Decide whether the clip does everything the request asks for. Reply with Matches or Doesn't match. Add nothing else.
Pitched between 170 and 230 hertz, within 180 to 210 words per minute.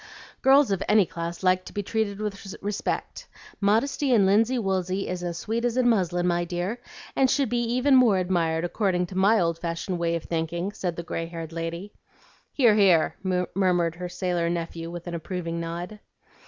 Matches